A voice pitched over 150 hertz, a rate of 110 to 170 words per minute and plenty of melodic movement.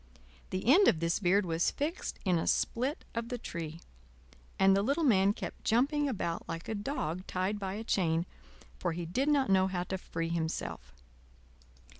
No: high, 190 Hz; average, 180 wpm; wide, 6.1 semitones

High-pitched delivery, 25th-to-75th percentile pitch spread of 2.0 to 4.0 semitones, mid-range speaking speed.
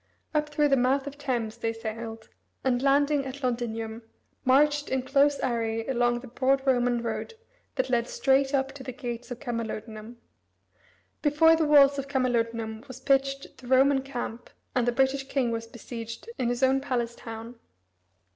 Yes: very high, 255 Hz; average, 2.8 semitones; average, 165 wpm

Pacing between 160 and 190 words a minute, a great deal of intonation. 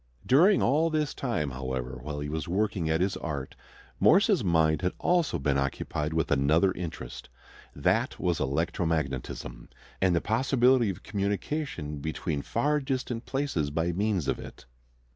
No: average, 145 wpm; wide, 8.9 semitones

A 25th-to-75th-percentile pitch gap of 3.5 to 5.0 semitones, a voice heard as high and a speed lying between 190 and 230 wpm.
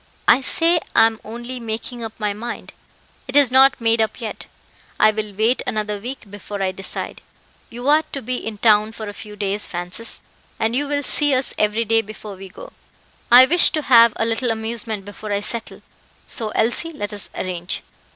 No: average, 3.0 semitones; high, 225 Hz; average, 195 wpm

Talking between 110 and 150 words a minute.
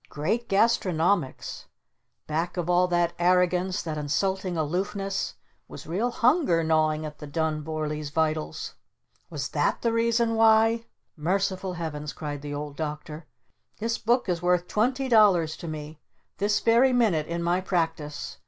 Yes: average, 145 wpm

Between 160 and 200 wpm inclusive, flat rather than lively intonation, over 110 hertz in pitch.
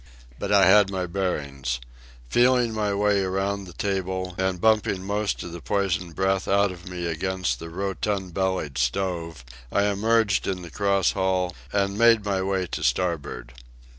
No: average, 165 wpm; narrow, 2.2 semitones; very low, 95 Hz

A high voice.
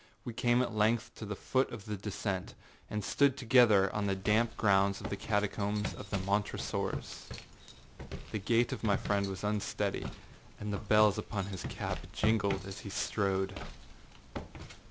No: low, 105 Hz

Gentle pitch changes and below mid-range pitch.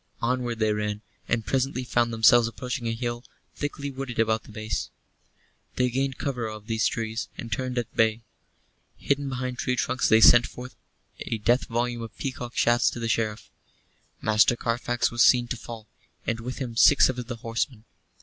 Yes: narrow, 2.0 semitones; low, 120 Hz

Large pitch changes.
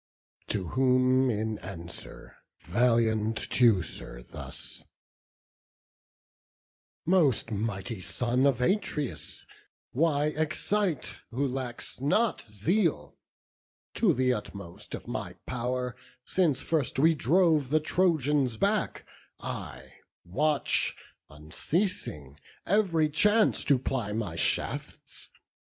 Yes: wide, 5.9 semitones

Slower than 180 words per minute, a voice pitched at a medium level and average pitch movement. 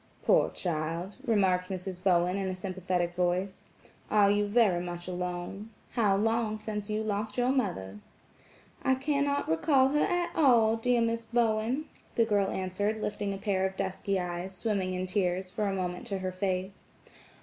No: average, 165 wpm; high, 195 Hz; average, 3.4 semitones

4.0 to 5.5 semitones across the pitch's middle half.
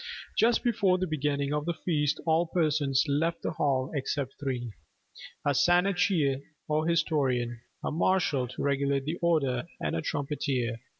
No: average, 3.6 semitones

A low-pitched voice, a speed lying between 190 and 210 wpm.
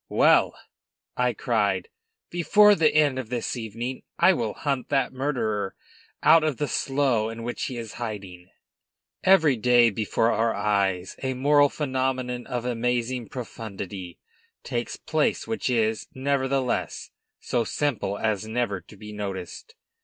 No: low, 120 Hz; average, 140 wpm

